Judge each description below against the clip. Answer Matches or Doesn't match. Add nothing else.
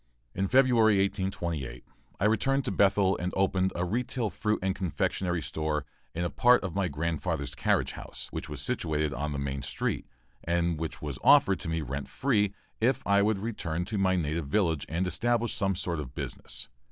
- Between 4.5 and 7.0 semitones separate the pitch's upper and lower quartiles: Matches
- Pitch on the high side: Doesn't match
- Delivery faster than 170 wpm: Matches